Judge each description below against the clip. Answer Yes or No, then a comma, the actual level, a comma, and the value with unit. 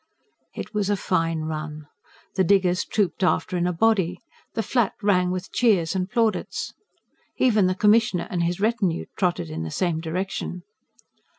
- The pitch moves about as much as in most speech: Yes, average, 3.4 semitones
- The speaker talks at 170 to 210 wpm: No, average, 160 wpm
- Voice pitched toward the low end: No, medium, 185 Hz